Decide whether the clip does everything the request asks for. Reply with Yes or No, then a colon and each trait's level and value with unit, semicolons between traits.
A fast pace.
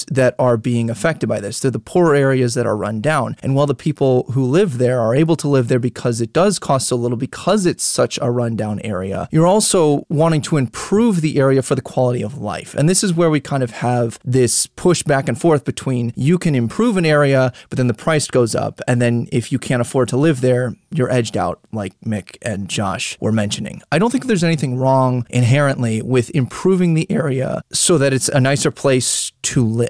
Yes: fast, 225 wpm